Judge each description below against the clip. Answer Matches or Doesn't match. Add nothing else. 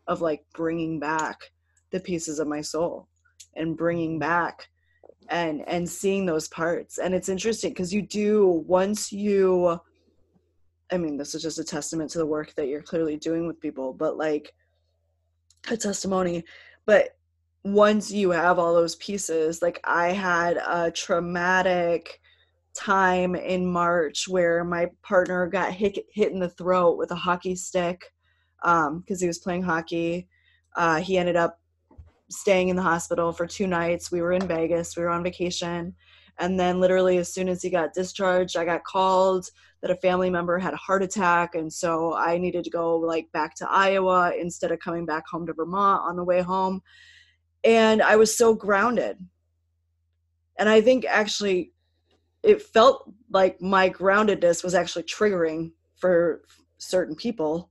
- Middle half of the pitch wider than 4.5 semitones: Doesn't match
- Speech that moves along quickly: Doesn't match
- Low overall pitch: Doesn't match